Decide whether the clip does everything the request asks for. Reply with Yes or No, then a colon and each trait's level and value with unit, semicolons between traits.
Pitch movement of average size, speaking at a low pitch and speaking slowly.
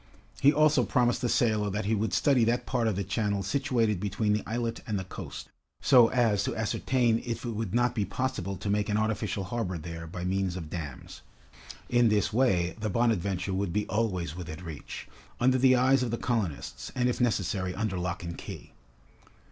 No: average, 4.2 semitones; low, 105 Hz; average, 195 wpm